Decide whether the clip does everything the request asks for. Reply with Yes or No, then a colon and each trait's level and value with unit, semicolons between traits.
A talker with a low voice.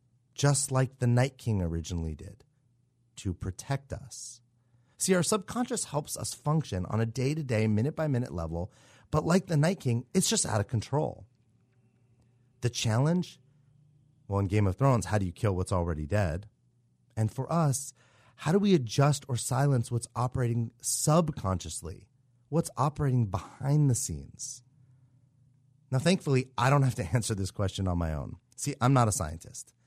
Yes: low, 125 Hz